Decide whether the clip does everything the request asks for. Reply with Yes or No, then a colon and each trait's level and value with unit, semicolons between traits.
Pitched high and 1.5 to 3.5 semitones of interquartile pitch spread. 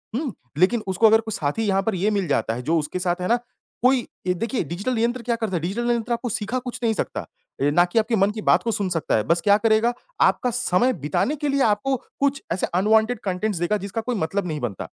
No: high, 215 Hz; average, 4.8 semitones